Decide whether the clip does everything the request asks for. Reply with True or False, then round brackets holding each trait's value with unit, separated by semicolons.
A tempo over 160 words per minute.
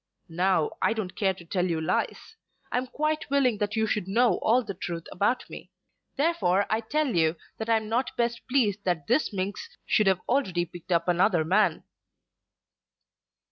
True (180 wpm)